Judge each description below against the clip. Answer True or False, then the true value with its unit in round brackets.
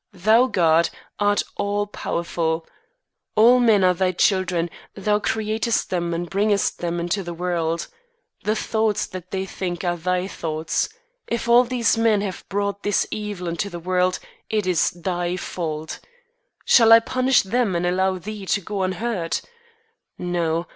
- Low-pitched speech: False (185 Hz)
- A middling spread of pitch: True (3.4 semitones)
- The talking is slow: False (155 wpm)